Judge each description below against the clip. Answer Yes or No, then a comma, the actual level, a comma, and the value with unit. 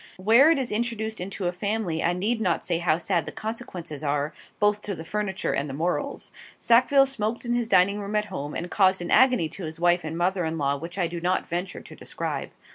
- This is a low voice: No, medium, 185 Hz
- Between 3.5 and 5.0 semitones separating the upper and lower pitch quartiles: Yes, average, 4.5 semitones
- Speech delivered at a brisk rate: Yes, fast, 230 wpm